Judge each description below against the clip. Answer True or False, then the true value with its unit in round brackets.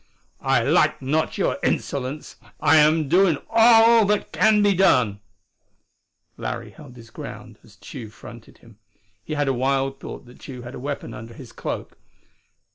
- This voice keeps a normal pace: True (160 wpm)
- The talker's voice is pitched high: False (135 Hz)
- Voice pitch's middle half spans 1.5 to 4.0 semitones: False (5.2 semitones)